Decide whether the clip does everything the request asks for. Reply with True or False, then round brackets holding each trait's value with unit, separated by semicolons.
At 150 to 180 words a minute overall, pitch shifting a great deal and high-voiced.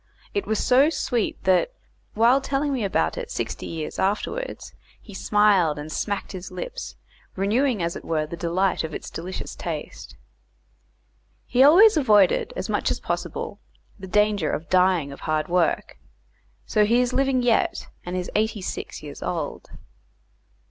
True (155 wpm; 6.4 semitones; 210 Hz)